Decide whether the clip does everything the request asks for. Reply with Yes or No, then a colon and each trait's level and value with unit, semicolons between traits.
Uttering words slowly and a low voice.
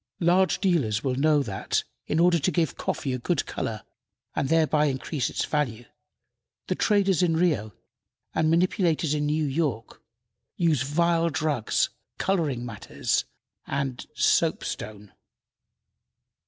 No: slow, 125 wpm; medium, 150 Hz